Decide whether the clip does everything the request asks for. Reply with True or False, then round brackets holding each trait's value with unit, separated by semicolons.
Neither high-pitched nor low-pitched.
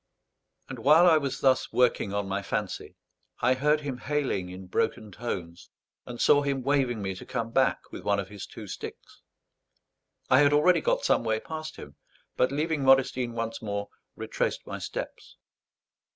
False (125 Hz)